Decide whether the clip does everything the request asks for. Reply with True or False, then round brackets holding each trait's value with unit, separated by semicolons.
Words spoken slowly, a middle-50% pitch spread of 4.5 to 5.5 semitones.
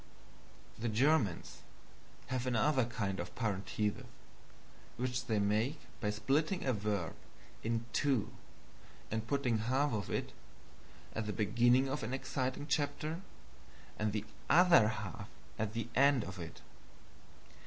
False (125 wpm; 4.1 semitones)